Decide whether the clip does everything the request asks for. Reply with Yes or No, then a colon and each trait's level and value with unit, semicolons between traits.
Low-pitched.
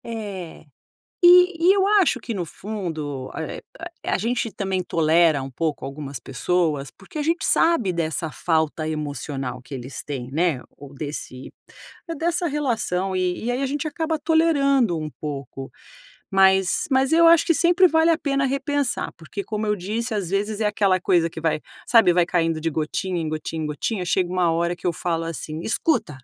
No: medium, 185 Hz